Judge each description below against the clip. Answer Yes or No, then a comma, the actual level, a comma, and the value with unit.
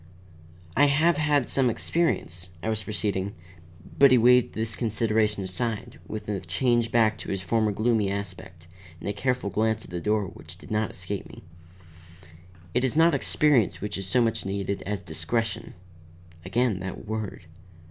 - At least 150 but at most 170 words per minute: Yes, average, 165 wpm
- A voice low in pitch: Yes, low, 110 Hz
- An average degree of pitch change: Yes, average, 3.5 semitones